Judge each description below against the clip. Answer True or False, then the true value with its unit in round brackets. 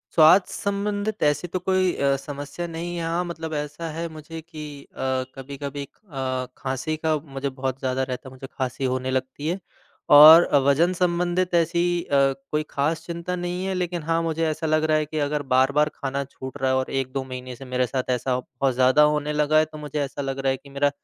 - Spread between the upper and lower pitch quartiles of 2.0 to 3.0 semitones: False (3.7 semitones)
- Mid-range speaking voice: True (150 Hz)